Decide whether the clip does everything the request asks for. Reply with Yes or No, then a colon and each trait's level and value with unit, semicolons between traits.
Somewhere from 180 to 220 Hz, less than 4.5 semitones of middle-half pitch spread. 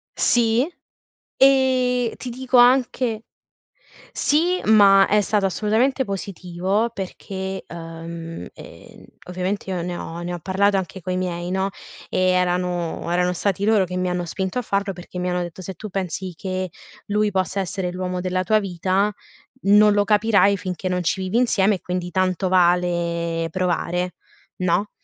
Yes: high, 190 Hz; narrow, 2.6 semitones